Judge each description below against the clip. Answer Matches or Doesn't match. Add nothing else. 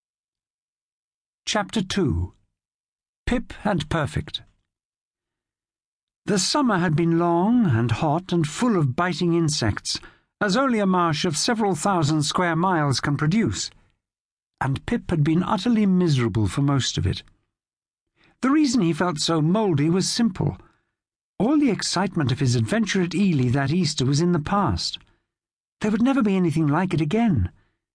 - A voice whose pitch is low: Doesn't match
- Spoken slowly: Doesn't match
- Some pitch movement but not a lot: Doesn't match